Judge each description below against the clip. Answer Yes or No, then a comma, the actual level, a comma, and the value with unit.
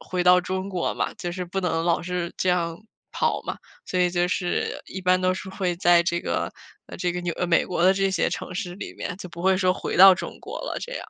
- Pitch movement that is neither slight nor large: No, narrow, 1.2 semitones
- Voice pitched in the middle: Yes, medium, 180 Hz